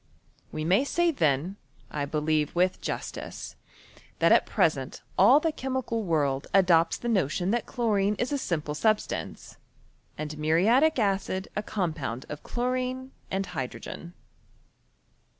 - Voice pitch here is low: No, high, 190 Hz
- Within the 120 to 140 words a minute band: Yes, slow, 135 wpm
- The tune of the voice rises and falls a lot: Yes, wide, 7.5 semitones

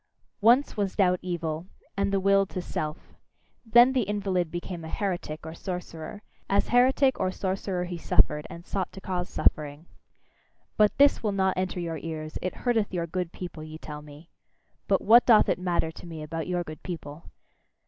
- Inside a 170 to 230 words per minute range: Yes, average, 180 wpm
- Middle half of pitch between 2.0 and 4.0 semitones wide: Yes, average, 3.5 semitones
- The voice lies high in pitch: No, medium, 180 Hz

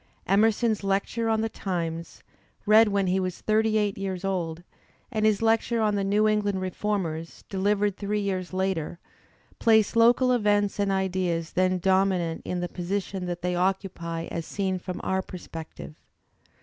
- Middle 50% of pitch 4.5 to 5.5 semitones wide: No, narrow, 2.6 semitones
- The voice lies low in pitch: No, high, 195 Hz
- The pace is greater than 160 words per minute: No, average, 155 wpm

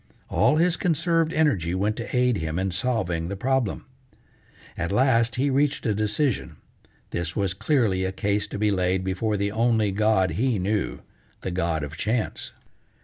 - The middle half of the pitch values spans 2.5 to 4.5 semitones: No, average, 5.1 semitones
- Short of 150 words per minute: No, average, 165 wpm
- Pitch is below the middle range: Yes, low, 105 Hz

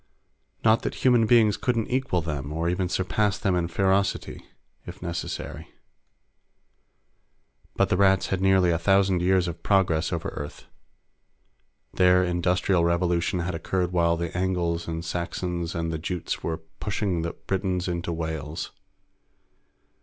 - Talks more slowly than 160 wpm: Yes, average, 140 wpm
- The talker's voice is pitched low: Yes, very low, 90 Hz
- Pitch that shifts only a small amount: Yes, narrow, 2.3 semitones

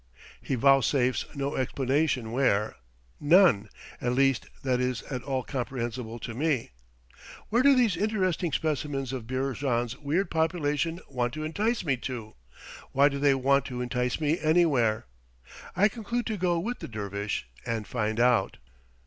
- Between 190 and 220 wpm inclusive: No, average, 150 wpm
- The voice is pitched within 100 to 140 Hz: Yes, low, 135 Hz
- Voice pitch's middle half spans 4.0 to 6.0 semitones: Yes, average, 4.7 semitones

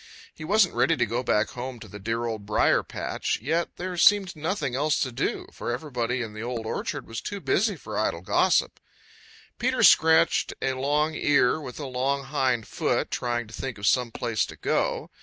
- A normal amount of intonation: Yes, average, 5.0 semitones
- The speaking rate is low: No, average, 195 wpm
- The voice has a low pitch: Yes, low, 130 Hz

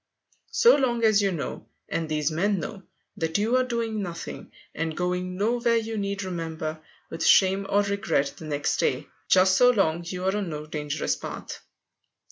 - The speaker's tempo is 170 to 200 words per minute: Yes, average, 175 wpm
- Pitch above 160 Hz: Yes, high, 190 Hz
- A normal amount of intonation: Yes, average, 4.8 semitones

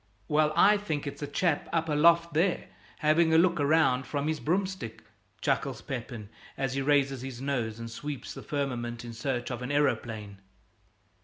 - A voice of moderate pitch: Yes, medium, 145 Hz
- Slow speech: No, average, 170 wpm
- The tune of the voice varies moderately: Yes, average, 4.5 semitones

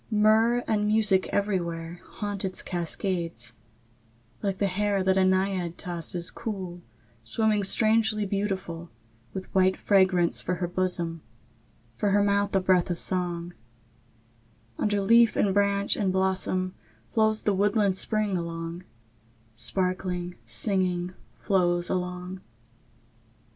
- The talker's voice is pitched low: No, high, 190 Hz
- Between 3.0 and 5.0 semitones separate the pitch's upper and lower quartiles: No, narrow, 2.4 semitones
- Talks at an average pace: No, slow, 120 wpm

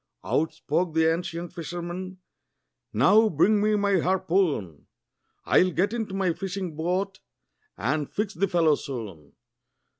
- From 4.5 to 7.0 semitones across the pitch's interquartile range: No, average, 3.5 semitones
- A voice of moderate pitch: Yes, medium, 175 Hz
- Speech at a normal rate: No, slow, 125 wpm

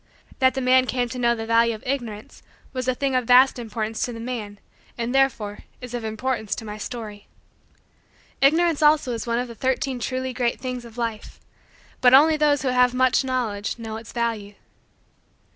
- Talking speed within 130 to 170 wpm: No, average, 190 wpm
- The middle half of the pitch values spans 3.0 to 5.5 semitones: No, narrow, 2.4 semitones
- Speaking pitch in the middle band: No, high, 245 Hz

